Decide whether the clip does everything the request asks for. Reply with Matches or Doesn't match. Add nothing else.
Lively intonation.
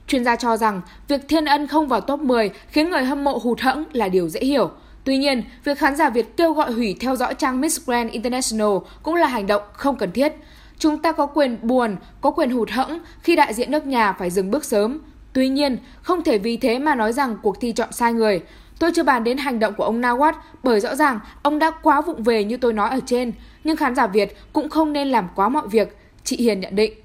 Doesn't match